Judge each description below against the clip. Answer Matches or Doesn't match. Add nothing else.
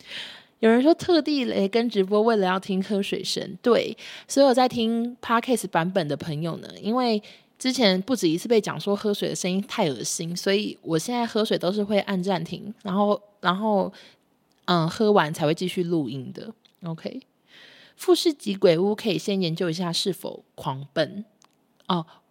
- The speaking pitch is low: Doesn't match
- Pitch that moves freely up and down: Doesn't match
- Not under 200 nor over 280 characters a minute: Matches